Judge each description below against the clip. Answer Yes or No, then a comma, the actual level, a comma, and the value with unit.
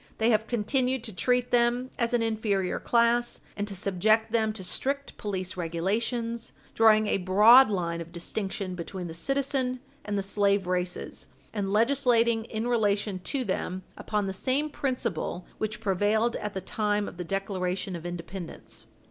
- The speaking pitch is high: Yes, high, 210 Hz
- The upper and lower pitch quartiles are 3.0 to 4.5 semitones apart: Yes, average, 3.9 semitones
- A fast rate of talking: No, average, 160 wpm